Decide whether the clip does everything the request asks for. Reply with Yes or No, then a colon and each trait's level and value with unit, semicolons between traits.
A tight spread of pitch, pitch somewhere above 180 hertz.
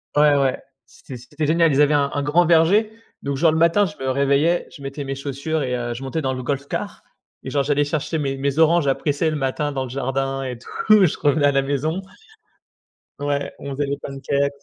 No: narrow, 2.3 semitones; medium, 140 Hz